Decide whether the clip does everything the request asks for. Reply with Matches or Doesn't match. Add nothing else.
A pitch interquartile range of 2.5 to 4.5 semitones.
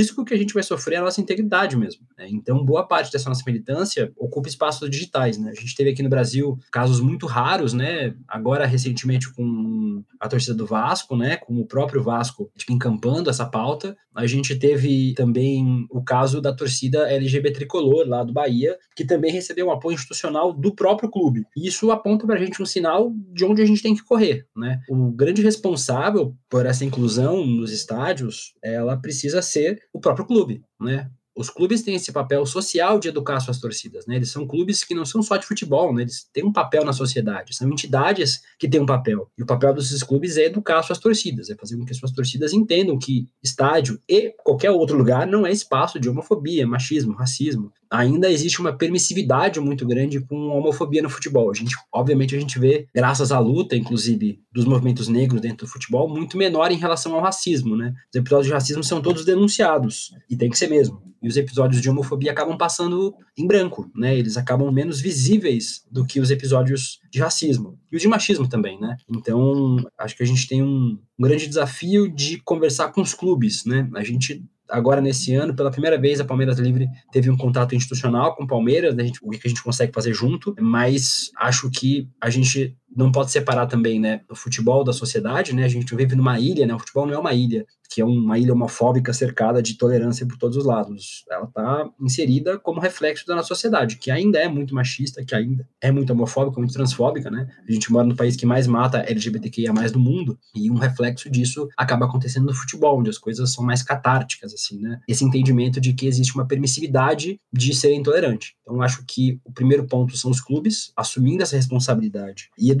Matches